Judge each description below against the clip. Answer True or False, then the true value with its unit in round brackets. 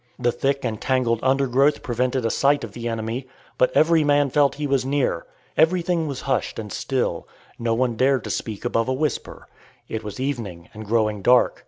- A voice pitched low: True (130 Hz)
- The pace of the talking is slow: False (190 wpm)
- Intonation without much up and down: False (3.3 semitones)